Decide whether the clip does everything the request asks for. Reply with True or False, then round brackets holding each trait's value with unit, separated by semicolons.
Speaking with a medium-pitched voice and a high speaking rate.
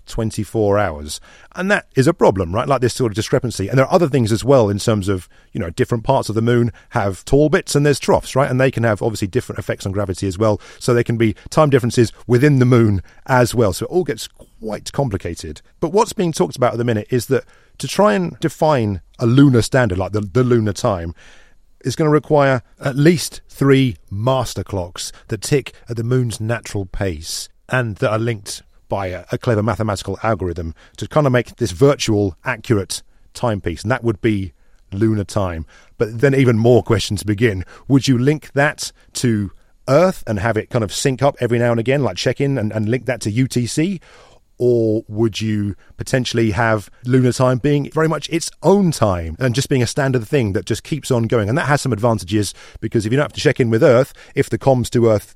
False (120 Hz; 220 wpm)